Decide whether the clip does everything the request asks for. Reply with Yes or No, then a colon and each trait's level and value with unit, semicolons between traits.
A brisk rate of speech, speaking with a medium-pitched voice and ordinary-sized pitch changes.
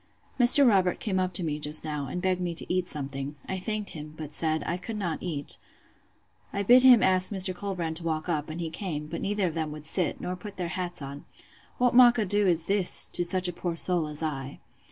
Yes: fast, 230 wpm; medium, 175 Hz; average, 3.7 semitones